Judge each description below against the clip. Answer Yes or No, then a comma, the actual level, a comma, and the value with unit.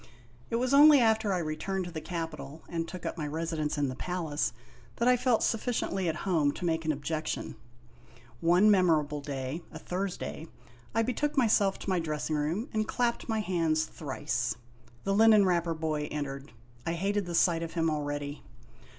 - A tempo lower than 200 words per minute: Yes, average, 180 wpm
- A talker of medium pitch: Yes, medium, 170 Hz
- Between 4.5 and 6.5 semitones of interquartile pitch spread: Yes, average, 4.8 semitones